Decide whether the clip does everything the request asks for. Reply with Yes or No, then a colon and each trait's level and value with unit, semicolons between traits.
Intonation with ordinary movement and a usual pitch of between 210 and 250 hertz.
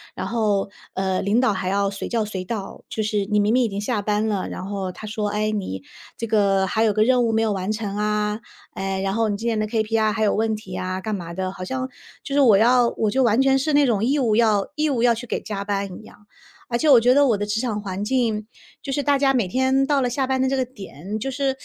Yes: average, 3.7 semitones; high, 215 Hz